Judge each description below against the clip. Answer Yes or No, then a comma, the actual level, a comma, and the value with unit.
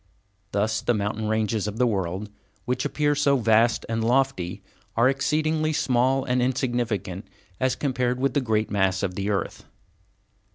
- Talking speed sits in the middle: Yes, average, 155 wpm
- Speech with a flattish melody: No, average, 3.9 semitones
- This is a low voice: Yes, low, 120 Hz